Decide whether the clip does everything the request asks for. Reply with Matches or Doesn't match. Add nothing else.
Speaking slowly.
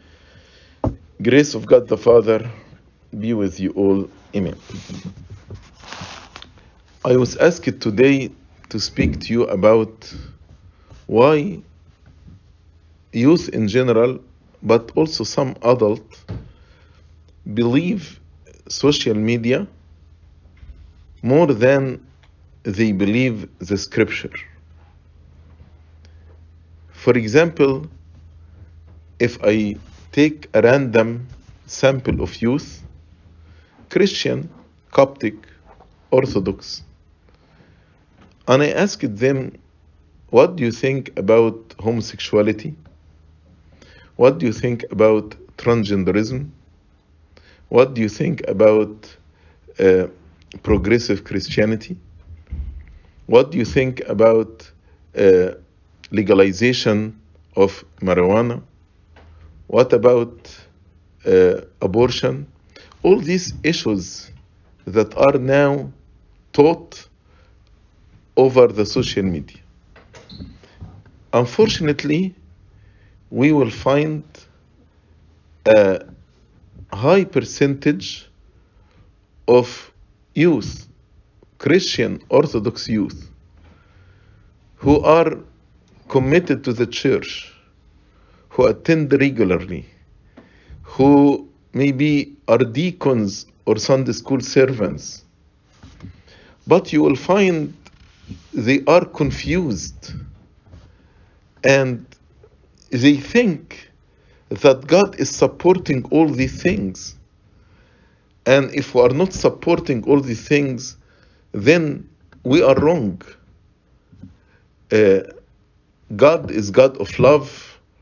Matches